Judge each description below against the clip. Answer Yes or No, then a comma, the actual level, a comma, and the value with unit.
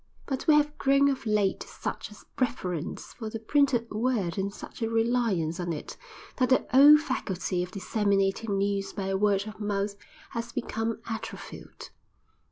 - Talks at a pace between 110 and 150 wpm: No, average, 165 wpm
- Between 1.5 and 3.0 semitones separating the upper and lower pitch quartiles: No, average, 4.2 semitones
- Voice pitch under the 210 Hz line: No, high, 215 Hz